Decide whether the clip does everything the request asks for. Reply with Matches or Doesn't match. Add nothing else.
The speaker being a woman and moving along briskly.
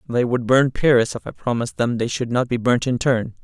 Doesn't match